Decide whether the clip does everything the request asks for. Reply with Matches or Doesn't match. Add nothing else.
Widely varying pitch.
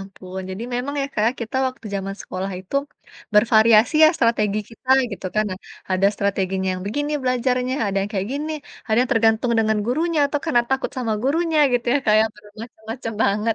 Doesn't match